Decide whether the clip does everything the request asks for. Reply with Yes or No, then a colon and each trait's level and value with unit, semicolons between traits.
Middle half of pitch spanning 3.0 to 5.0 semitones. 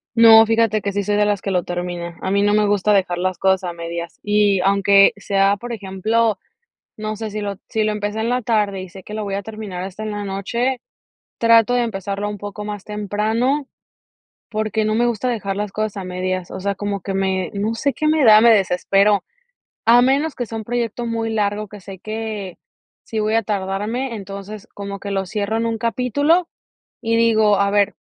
No: narrow, 2.4 semitones